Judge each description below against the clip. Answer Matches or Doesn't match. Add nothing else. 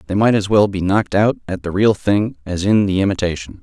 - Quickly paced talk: Matches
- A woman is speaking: Doesn't match